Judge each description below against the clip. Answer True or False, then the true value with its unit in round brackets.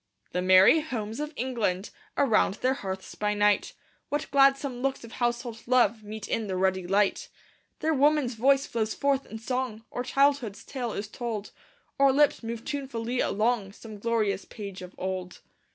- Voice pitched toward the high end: True (230 Hz)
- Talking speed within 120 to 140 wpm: False (165 wpm)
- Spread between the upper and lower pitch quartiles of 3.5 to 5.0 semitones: True (4.4 semitones)